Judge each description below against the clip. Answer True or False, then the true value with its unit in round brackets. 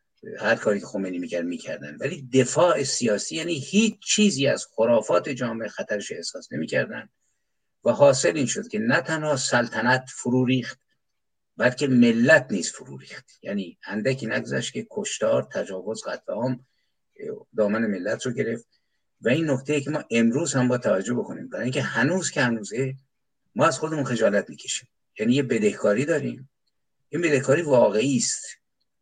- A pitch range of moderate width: True (4.5 semitones)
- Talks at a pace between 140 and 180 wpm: True (150 wpm)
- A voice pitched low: True (130 Hz)